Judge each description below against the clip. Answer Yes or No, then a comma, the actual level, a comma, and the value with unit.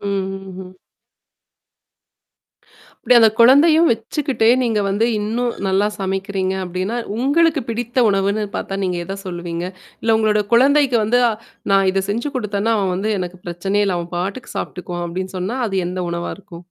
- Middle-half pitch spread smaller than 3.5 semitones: No, average, 3.9 semitones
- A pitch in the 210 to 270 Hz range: No, high, 200 Hz